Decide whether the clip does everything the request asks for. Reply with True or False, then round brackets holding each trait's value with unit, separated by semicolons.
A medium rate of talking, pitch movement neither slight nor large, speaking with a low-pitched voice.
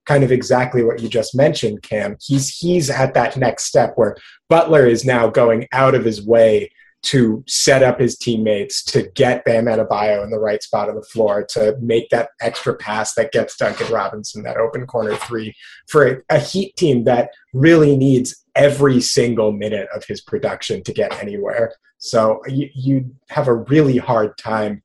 True (185 wpm; 3.7 semitones; 125 Hz)